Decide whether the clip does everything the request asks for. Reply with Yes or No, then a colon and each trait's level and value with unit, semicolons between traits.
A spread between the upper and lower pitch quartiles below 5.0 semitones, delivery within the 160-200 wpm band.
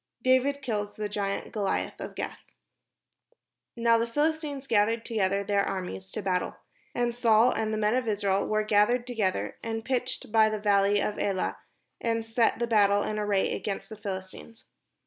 Yes: narrow, 2.5 semitones; average, 165 wpm